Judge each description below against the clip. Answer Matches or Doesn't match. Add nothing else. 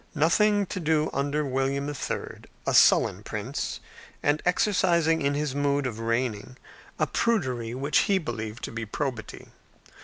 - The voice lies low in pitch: Doesn't match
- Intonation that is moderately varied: Matches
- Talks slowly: Doesn't match